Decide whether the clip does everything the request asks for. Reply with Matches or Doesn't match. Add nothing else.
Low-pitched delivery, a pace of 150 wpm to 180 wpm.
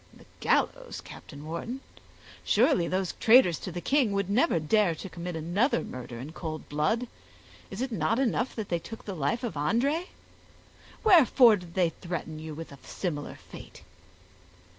Doesn't match